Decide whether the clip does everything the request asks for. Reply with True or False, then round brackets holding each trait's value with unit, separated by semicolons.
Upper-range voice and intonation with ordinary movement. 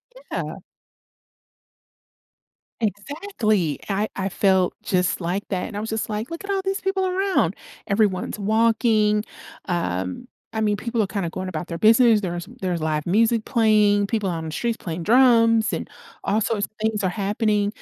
True (210 Hz; 3.5 semitones)